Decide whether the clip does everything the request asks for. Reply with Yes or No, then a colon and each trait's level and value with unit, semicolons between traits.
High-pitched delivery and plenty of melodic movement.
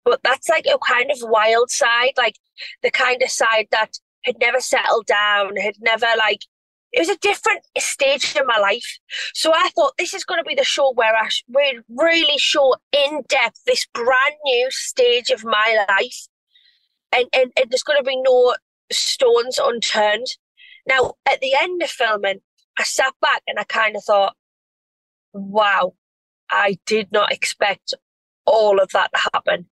Yes: very high, 265 Hz; wide, 7.0 semitones